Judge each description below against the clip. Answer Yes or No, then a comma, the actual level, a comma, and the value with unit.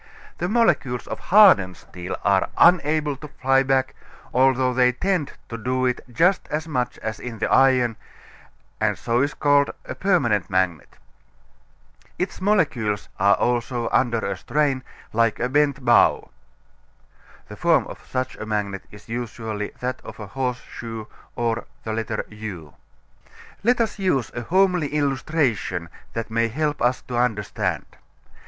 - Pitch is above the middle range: No, low, 125 Hz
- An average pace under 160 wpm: Yes, average, 145 wpm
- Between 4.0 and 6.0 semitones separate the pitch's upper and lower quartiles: Yes, average, 4.7 semitones